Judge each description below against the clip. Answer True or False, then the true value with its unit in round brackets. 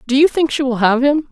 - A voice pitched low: False (270 Hz)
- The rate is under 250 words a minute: False (320 wpm)